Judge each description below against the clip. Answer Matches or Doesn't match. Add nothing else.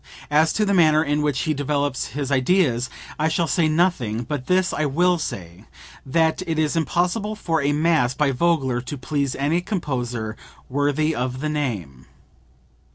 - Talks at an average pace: Matches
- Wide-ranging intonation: Doesn't match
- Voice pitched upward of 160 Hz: Doesn't match